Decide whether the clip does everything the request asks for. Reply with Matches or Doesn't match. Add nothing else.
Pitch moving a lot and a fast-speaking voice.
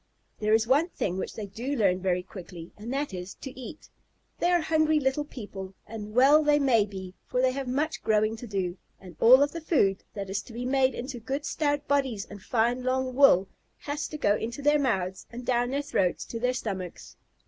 Matches